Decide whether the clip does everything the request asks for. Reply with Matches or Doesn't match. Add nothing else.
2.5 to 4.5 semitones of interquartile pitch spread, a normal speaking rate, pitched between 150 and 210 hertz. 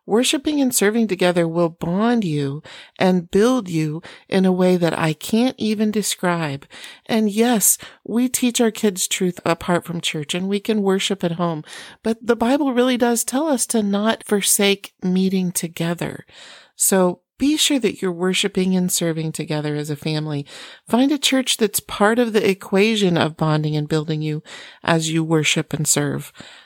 Doesn't match